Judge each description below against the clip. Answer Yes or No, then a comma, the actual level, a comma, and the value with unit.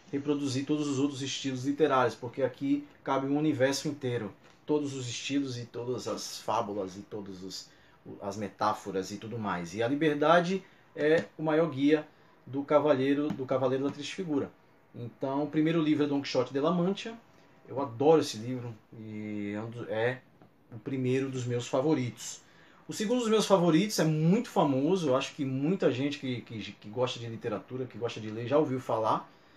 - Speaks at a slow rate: No, average, 175 wpm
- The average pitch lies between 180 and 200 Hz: No, medium, 140 Hz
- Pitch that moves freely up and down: No, average, 4.3 semitones